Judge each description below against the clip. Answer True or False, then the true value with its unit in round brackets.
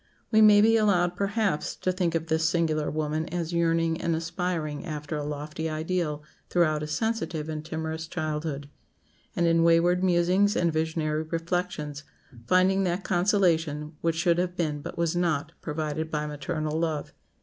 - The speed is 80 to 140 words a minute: False (160 wpm)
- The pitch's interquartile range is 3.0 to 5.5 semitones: False (2.5 semitones)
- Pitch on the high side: False (165 Hz)